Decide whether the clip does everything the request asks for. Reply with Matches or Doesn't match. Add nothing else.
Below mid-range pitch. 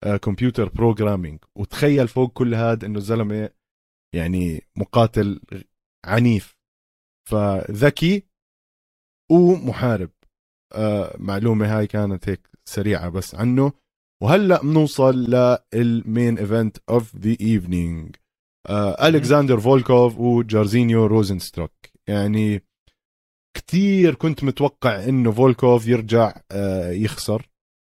Matches